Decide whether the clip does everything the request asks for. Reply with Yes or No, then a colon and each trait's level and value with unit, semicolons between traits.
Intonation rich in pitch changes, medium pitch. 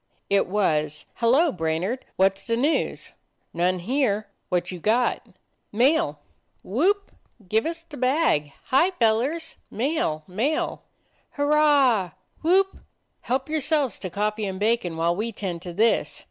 No: wide, 7.9 semitones; high, 225 Hz